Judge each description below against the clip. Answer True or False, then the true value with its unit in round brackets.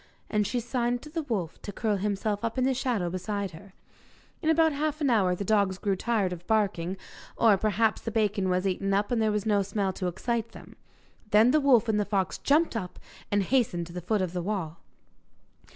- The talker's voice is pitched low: False (210 Hz)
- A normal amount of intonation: True (3.8 semitones)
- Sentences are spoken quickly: True (215 wpm)